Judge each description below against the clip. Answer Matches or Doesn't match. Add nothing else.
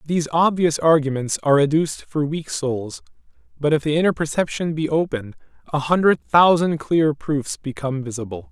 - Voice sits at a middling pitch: Matches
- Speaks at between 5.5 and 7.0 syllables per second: Doesn't match